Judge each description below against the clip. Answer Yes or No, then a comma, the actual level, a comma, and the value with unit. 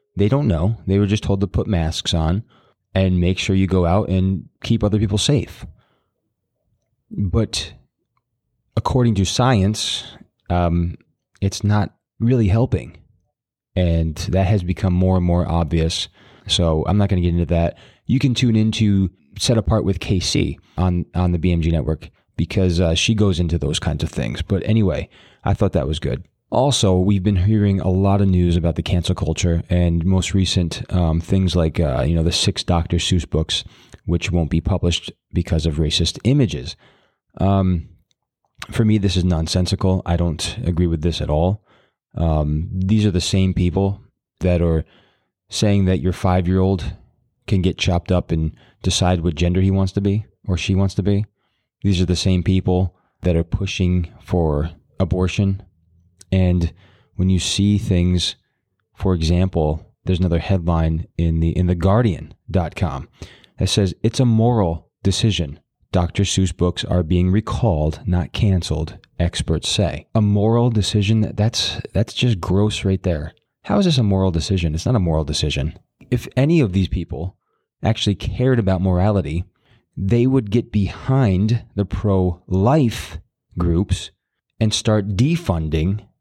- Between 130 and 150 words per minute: No, average, 160 wpm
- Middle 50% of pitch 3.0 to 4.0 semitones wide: Yes, average, 3.3 semitones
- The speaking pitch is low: Yes, very low, 95 Hz